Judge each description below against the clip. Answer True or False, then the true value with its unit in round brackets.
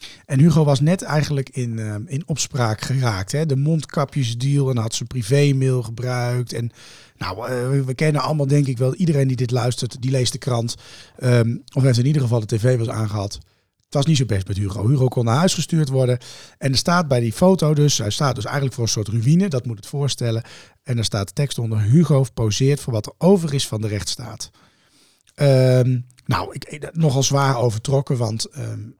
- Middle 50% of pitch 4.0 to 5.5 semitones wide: False (3.6 semitones)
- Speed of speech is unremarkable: False (205 wpm)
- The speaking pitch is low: True (130 Hz)